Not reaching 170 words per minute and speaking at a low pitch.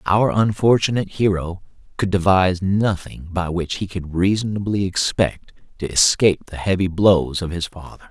Yes: average, 150 wpm; very low, 95 Hz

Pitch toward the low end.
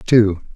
Yes: low, 105 Hz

